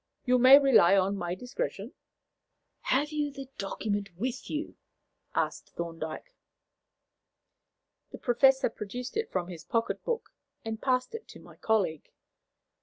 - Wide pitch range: Yes, wide, 5.8 semitones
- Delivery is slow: Yes, slow, 130 wpm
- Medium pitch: No, high, 240 Hz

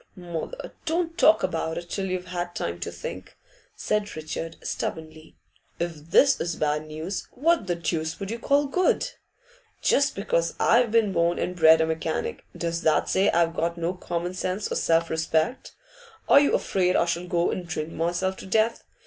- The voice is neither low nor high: Yes, medium, 175 Hz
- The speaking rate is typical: Yes, average, 180 wpm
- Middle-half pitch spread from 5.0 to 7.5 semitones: No, average, 3.6 semitones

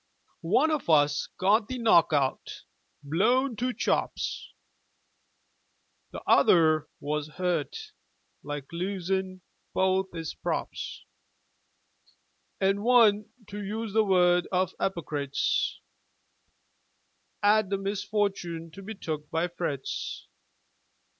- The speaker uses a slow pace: Yes, slow, 95 wpm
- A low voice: No, high, 190 Hz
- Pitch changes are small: No, average, 4.2 semitones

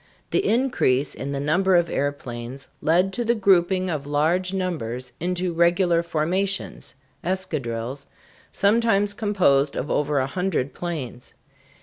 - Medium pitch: Yes, medium, 170 Hz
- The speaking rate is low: Yes, slow, 125 wpm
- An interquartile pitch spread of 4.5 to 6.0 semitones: Yes, average, 5.2 semitones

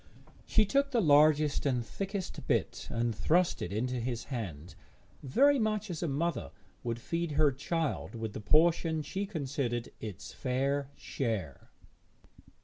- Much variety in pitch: Yes, wide, 6.2 semitones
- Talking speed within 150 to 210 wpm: No, average, 140 wpm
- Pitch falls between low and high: Yes, medium, 145 Hz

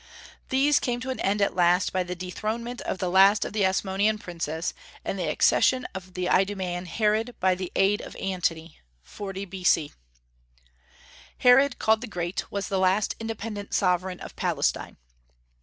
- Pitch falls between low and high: No, high, 195 Hz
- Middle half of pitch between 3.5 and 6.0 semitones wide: No, average, 3.0 semitones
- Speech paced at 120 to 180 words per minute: Yes, average, 160 wpm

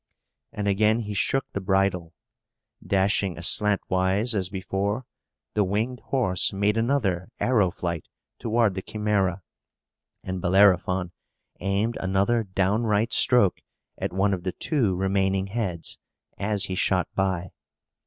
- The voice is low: Yes, low, 100 Hz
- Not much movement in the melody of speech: Yes, narrow, 2.3 semitones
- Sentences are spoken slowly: Yes, slow, 125 wpm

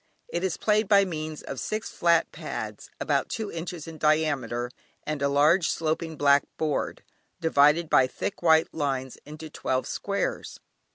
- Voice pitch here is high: No, medium, 155 Hz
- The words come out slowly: No, average, 155 wpm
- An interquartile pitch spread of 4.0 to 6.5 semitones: No, average, 3.1 semitones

